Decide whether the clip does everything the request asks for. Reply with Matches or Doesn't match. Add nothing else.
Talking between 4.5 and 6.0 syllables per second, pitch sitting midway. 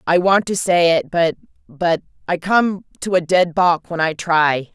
Doesn't match